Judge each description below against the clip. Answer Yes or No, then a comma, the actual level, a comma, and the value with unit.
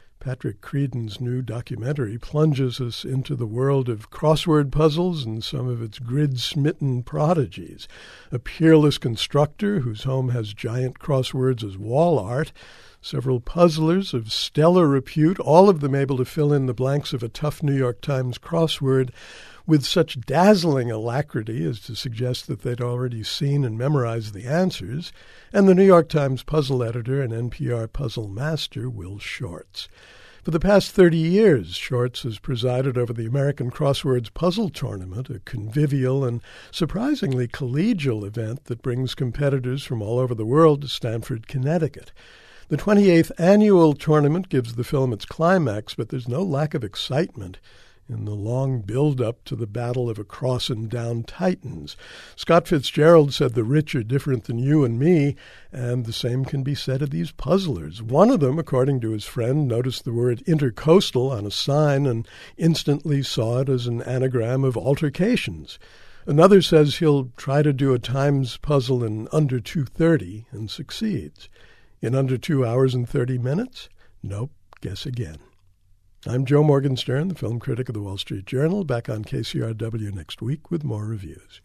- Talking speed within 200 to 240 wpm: No, average, 165 wpm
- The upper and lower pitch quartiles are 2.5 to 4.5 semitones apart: Yes, average, 4.1 semitones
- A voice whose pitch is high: No, low, 130 Hz